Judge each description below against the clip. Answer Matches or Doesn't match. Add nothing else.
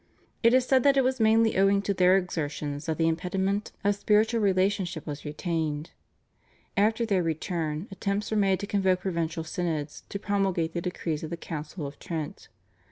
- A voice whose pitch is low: Doesn't match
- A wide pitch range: Doesn't match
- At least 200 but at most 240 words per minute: Doesn't match